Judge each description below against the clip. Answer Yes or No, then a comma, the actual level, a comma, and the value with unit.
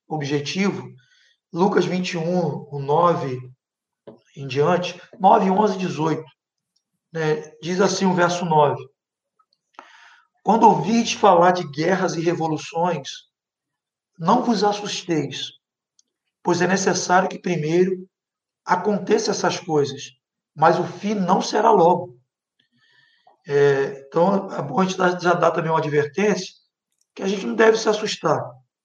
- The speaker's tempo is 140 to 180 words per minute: No, average, 125 wpm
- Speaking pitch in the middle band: Yes, medium, 180 Hz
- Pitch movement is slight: No, average, 4.2 semitones